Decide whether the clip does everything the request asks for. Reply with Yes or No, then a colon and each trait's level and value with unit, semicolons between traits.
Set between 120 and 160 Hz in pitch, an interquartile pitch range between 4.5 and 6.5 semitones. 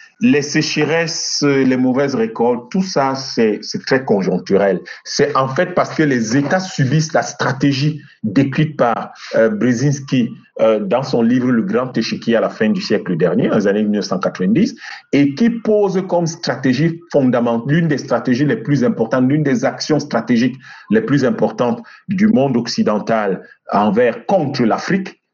Yes: medium, 140 Hz; average, 5.1 semitones